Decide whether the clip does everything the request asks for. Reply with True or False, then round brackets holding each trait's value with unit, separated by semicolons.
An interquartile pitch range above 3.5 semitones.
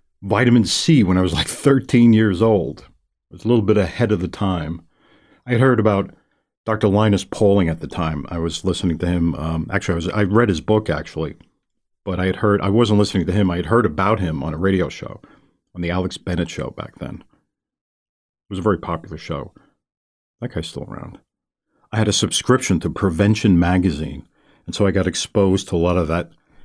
True (4.0 semitones)